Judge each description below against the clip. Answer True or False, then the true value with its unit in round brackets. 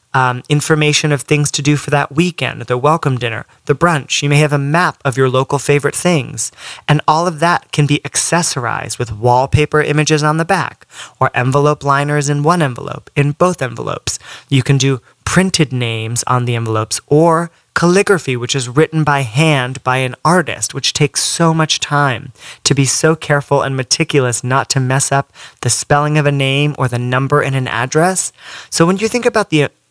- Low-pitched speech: False (145 Hz)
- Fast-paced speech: False (195 wpm)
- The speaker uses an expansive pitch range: False (3.1 semitones)